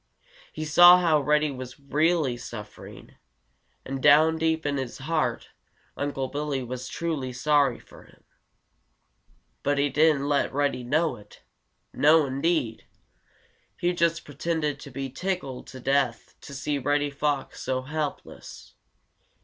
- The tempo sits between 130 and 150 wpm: Yes, slow, 135 wpm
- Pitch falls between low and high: Yes, medium, 145 Hz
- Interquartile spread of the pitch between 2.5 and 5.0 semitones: Yes, average, 2.8 semitones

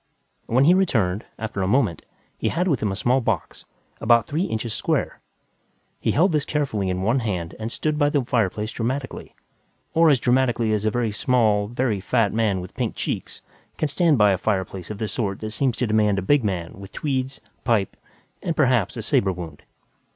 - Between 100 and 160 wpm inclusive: No, average, 195 wpm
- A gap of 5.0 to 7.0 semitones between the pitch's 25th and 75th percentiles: No, average, 4.6 semitones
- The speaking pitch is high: No, low, 115 Hz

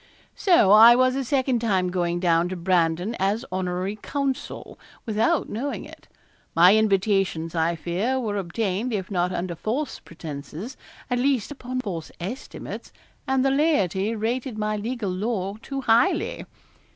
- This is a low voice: No, high, 210 Hz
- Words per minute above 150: No, average, 145 wpm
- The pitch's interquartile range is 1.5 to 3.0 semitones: No, wide, 5.6 semitones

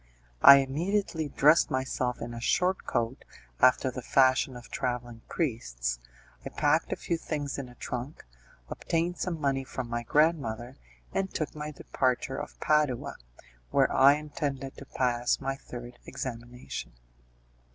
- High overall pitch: No, low, 135 Hz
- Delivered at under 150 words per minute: Yes, average, 140 wpm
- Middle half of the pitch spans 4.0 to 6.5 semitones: No, average, 3.6 semitones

